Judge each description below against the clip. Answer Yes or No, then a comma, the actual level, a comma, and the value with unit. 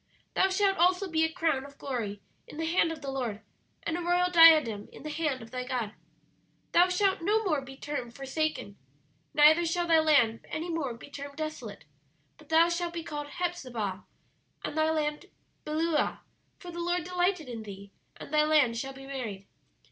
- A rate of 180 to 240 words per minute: Yes, average, 185 wpm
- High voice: Yes, very high, 305 Hz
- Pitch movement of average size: Yes, average, 4.5 semitones